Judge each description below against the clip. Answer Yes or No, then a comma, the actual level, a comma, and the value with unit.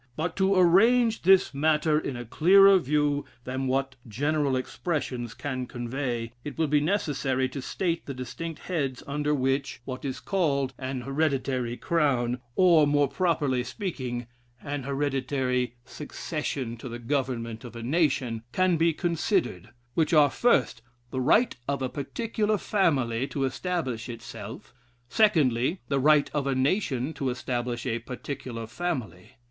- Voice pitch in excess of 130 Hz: Yes, medium, 140 Hz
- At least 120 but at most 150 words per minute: Yes, average, 145 wpm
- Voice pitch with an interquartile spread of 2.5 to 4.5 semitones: Yes, average, 4.2 semitones